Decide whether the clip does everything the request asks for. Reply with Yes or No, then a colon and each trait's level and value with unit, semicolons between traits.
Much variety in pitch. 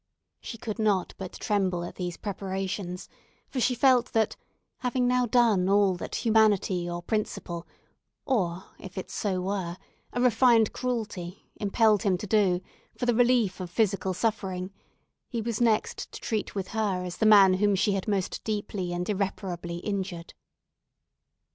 No: average, 3.4 semitones